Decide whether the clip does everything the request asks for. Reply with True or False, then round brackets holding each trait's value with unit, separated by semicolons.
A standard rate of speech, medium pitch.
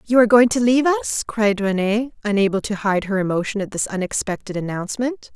False (190 wpm; 215 Hz)